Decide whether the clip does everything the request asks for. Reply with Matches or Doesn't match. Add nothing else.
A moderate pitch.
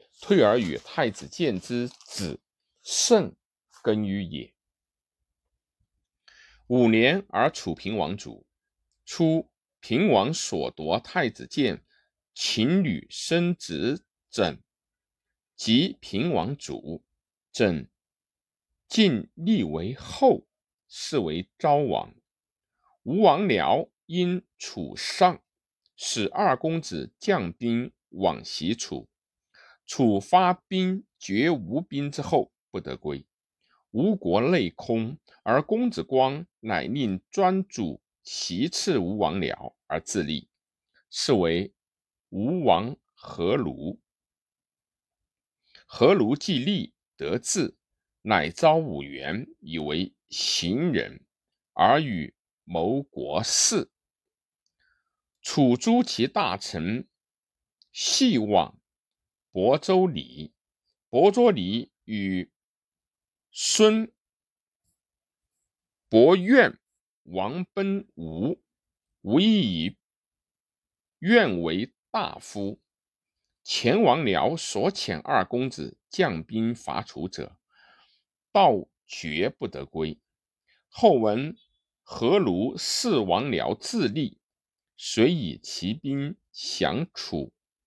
Matches